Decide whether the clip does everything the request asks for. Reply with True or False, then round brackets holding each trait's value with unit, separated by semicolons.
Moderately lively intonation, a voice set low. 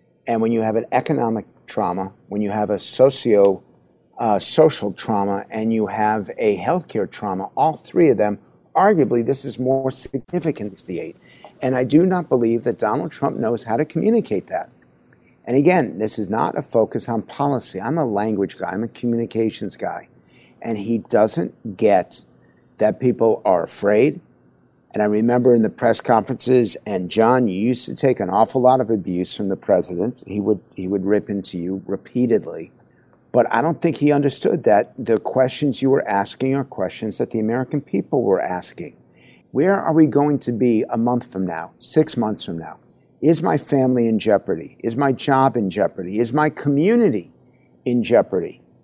True (4.1 semitones; 115 Hz)